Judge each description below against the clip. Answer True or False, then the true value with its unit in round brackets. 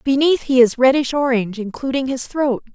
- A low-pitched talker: False (260 Hz)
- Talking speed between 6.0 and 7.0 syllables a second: False (5.5 syllables/s)